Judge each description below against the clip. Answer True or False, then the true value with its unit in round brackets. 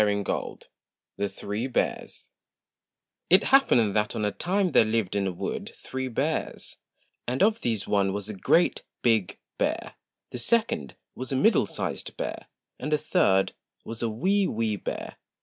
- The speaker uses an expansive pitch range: True (7.0 semitones)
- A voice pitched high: False (115 Hz)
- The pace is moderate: True (165 wpm)